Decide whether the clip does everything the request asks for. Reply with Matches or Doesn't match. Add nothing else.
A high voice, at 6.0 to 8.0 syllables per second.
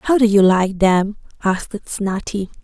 Doesn't match